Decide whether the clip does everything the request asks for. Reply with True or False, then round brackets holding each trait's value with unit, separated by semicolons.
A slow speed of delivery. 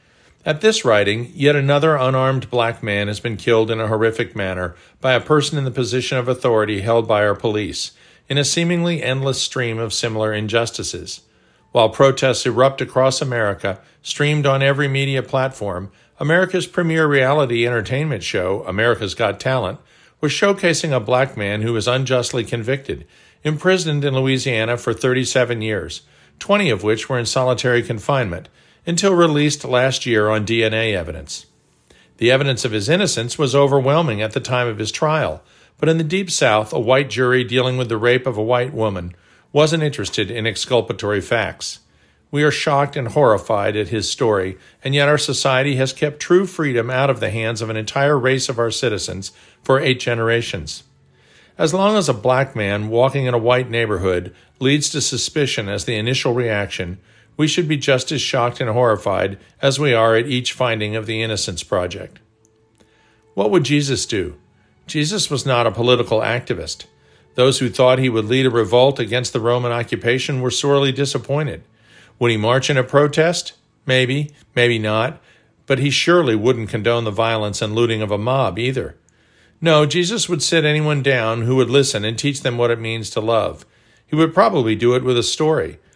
False (175 wpm)